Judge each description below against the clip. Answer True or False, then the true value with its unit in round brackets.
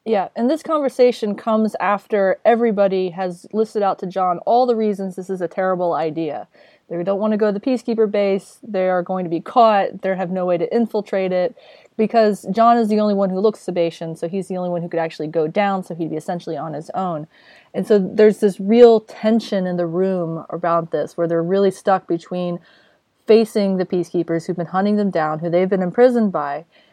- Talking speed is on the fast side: True (215 wpm)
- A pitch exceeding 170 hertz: True (190 Hz)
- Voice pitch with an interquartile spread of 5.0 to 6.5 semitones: False (3.6 semitones)